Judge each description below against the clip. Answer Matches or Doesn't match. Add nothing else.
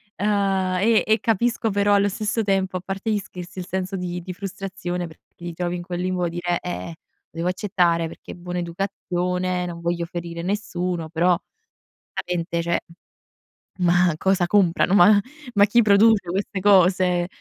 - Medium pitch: Matches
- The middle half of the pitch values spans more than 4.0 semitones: Doesn't match